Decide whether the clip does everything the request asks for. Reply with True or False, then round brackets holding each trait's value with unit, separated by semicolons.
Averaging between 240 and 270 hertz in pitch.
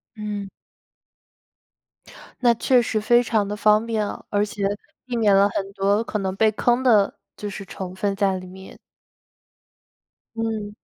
False (210 Hz)